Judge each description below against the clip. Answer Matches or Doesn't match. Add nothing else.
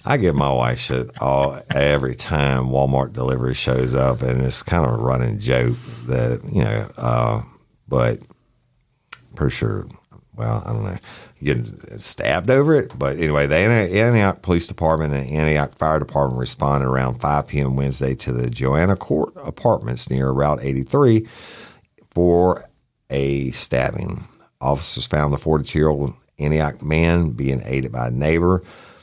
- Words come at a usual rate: Matches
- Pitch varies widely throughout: Doesn't match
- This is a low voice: Matches